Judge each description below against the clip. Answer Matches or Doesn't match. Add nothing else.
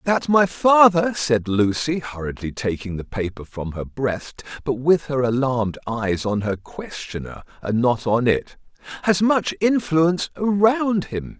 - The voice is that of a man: Matches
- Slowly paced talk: Doesn't match